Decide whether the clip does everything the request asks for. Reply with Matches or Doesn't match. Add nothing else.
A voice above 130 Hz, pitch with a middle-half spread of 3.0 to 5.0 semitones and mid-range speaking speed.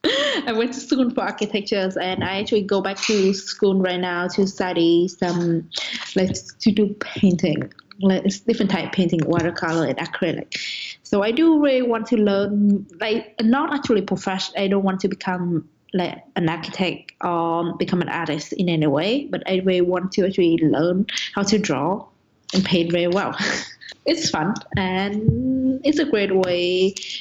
Matches